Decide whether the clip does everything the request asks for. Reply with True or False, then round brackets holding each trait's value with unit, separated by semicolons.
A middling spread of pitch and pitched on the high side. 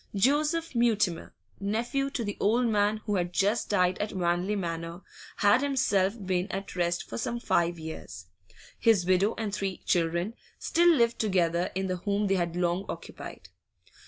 True (4.2 semitones; 195 Hz)